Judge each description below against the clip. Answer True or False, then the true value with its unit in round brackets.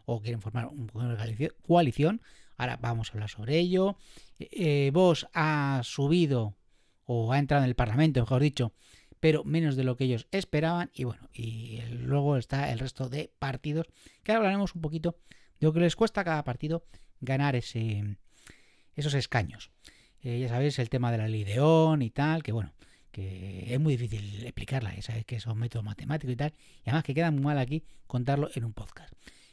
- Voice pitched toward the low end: True (130 Hz)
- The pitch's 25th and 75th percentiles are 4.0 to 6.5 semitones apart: True (5.2 semitones)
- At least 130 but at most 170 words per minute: False (185 wpm)